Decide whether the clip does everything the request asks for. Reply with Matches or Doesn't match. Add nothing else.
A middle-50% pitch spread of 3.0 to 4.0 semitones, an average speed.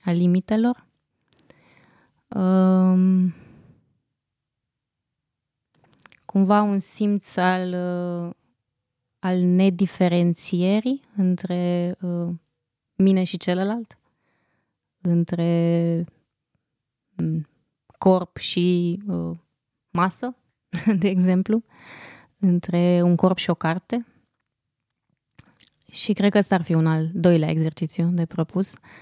Doesn't match